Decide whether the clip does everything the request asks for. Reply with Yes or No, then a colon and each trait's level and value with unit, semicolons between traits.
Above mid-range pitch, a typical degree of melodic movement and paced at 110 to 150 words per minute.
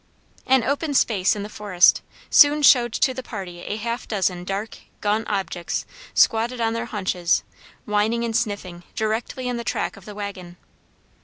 No: high, 215 Hz; average, 3.3 semitones; average, 165 wpm